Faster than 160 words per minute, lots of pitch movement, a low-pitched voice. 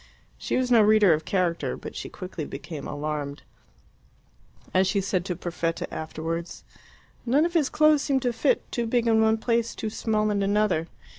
No: average, 175 wpm; wide, 5.8 semitones; high, 205 Hz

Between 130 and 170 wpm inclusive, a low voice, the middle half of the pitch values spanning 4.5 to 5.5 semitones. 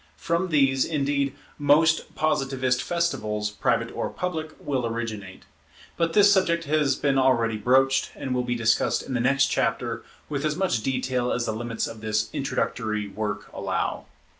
Yes: average, 160 wpm; low, 130 Hz; average, 4.9 semitones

